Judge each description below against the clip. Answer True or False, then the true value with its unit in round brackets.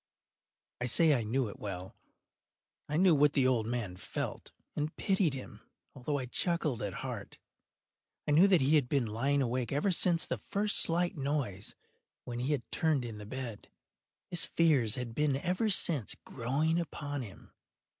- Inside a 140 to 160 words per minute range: False (170 wpm)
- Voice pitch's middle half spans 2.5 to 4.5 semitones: False (5.1 semitones)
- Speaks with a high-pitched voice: False (140 Hz)